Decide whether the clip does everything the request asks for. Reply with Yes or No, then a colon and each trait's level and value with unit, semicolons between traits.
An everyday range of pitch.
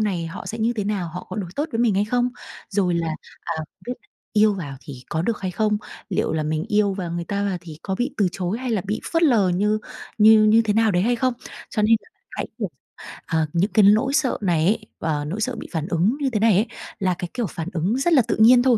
Yes: average, 4.4 semitones